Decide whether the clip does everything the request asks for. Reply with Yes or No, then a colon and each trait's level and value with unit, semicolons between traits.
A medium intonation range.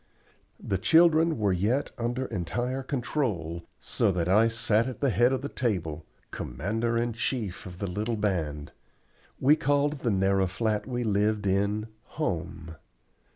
Yes: average, 5.0 semitones